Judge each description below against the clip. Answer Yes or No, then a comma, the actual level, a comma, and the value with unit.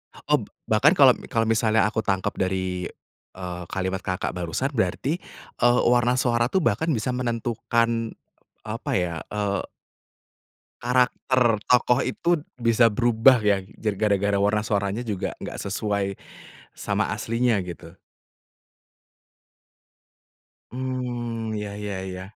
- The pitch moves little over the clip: No, average, 3.6 semitones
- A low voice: Yes, low, 110 Hz